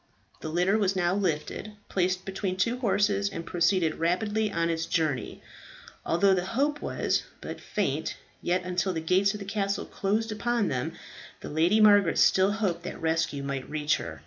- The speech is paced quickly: No, average, 170 wpm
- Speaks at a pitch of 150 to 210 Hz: Yes, medium, 185 Hz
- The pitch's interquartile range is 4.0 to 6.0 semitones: No, average, 3.6 semitones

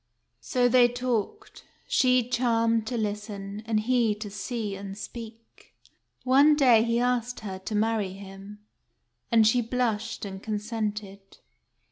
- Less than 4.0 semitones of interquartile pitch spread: Yes, average, 2.8 semitones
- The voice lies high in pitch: Yes, high, 225 Hz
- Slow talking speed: Yes, slow, 130 wpm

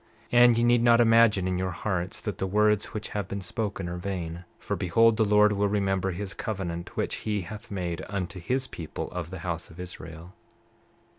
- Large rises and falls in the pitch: No, average, 3.2 semitones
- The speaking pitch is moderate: No, very low, 95 Hz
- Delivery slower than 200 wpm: No, fast, 205 wpm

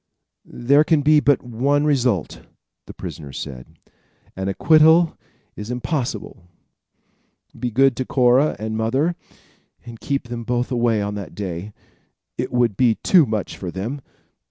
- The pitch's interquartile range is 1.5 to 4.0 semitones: No, average, 4.8 semitones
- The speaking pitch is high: No, low, 120 Hz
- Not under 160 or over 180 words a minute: No, average, 140 wpm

